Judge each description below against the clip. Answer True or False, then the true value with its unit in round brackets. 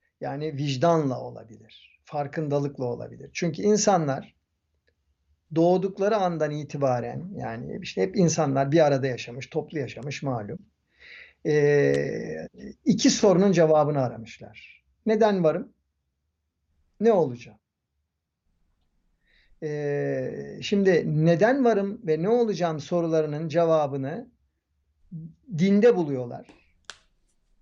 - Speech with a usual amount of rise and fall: False (7.3 semitones)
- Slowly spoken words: True (85 wpm)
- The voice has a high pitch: False (145 Hz)